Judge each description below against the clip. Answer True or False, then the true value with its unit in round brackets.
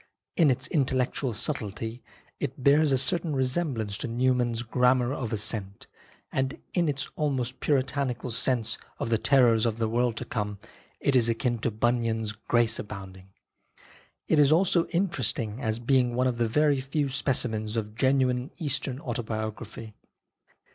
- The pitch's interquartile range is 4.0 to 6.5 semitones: False (3.3 semitones)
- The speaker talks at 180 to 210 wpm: False (145 wpm)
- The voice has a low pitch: True (125 Hz)